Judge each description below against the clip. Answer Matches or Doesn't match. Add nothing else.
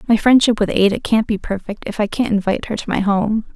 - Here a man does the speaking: Doesn't match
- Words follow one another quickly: Matches